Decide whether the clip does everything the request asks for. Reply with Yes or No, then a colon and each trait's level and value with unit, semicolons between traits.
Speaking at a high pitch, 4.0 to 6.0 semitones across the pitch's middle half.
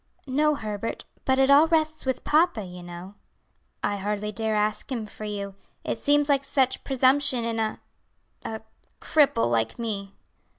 Yes: high, 225 Hz; wide, 5.4 semitones